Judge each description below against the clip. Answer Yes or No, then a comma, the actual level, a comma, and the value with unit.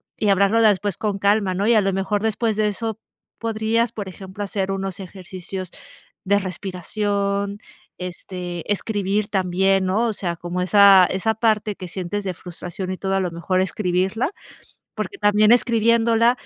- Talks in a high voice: Yes, high, 200 Hz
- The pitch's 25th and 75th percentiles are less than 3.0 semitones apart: Yes, narrow, 2.4 semitones